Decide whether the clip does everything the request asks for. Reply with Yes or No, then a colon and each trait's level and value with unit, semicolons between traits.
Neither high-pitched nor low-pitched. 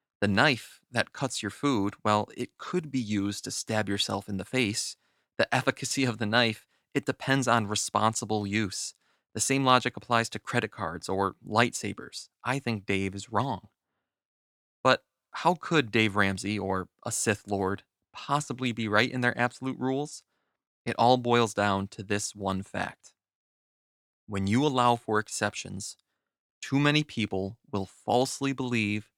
No: low, 110 Hz